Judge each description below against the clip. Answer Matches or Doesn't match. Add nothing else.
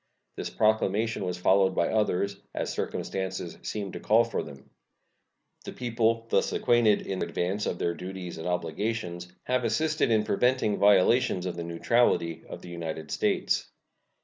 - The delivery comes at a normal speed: Matches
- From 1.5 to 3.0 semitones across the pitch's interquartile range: Doesn't match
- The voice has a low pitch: Matches